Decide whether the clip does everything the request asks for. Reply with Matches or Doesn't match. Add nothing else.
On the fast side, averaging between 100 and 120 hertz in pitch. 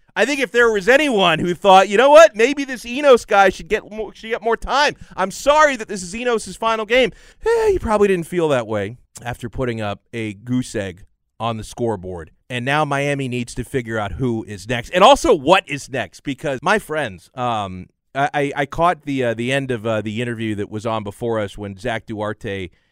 Doesn't match